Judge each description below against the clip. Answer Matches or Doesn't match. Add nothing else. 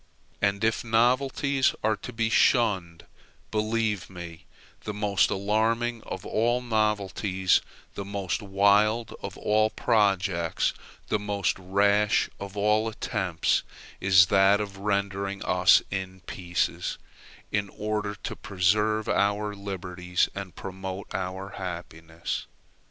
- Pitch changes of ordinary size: Doesn't match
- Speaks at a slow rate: Matches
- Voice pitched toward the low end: Matches